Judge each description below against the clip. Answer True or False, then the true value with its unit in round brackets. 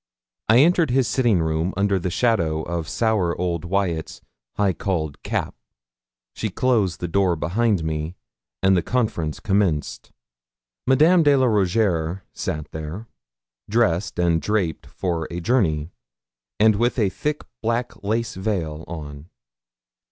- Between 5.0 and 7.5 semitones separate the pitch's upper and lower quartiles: True (5.5 semitones)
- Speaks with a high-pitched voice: False (95 Hz)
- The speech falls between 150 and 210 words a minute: False (135 wpm)